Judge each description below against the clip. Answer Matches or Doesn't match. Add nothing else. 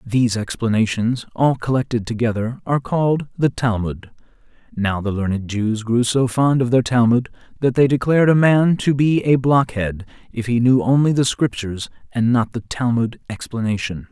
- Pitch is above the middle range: Doesn't match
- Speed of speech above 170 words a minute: Doesn't match